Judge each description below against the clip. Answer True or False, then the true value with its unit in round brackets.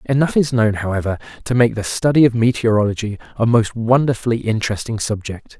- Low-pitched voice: True (115 Hz)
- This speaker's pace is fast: False (160 wpm)